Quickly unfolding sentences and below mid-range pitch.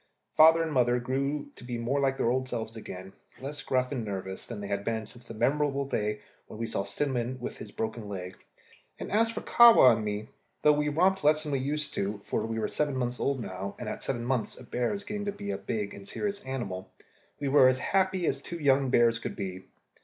Yes: fast, 235 wpm; low, 125 Hz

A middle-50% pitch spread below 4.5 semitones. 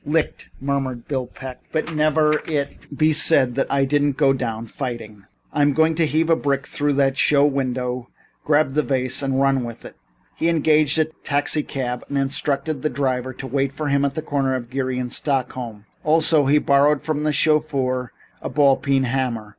Yes: narrow, 2.6 semitones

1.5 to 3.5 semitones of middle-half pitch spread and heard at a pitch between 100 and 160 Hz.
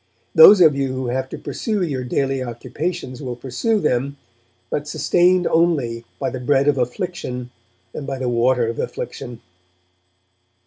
No: average, 4.4 semitones; low, 135 Hz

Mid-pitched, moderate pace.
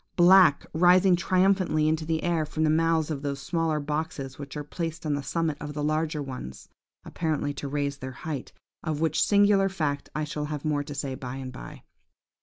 Yes: medium, 155 Hz; average, 195 wpm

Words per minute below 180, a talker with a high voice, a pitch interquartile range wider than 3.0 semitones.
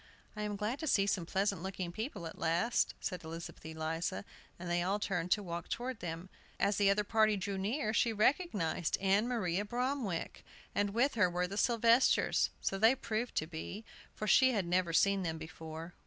No: average, 190 wpm; high, 195 Hz; average, 4.1 semitones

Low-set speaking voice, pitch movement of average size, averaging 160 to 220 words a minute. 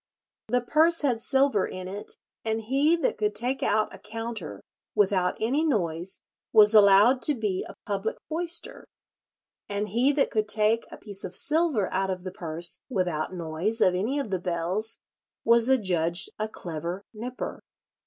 No: high, 210 Hz; average, 5.0 semitones; average, 165 wpm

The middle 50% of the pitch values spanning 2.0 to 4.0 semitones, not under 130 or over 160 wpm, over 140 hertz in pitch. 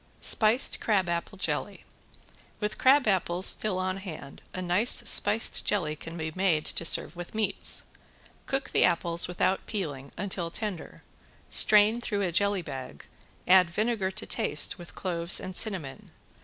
Yes: average, 3.6 semitones; average, 140 wpm; medium, 185 Hz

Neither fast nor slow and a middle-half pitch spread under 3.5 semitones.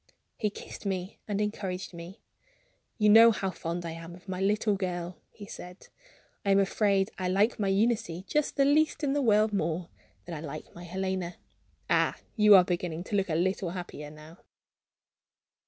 Yes: average, 180 wpm; average, 3.1 semitones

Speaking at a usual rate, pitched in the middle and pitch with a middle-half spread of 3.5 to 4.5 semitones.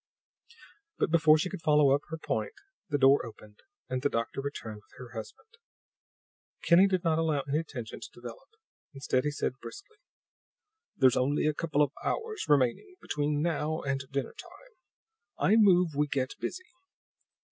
Yes: average, 160 wpm; medium, 150 Hz; average, 4.2 semitones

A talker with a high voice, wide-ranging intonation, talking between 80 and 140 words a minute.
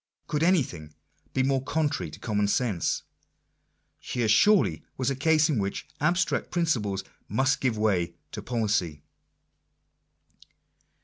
No: low, 125 Hz; wide, 6.6 semitones; slow, 135 wpm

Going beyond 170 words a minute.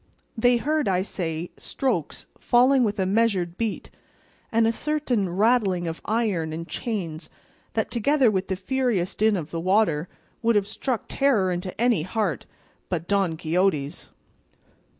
No: average, 150 wpm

